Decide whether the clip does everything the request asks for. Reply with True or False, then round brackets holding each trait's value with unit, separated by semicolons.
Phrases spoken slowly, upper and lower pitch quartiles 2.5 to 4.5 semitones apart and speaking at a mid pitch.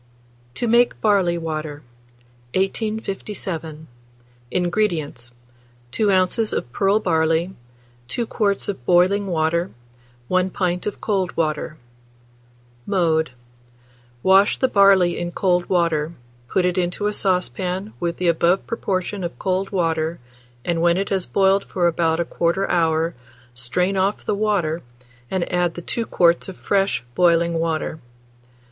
True (130 wpm; 2.9 semitones; 180 Hz)